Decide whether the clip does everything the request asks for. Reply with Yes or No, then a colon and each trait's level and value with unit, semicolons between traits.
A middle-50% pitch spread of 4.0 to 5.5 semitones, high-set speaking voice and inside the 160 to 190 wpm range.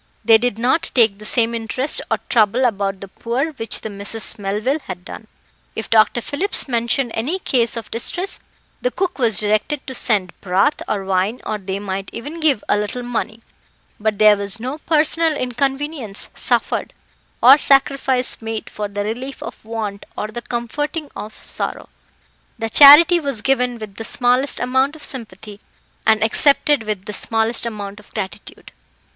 Yes: average, 4.4 semitones; high, 230 Hz; average, 165 wpm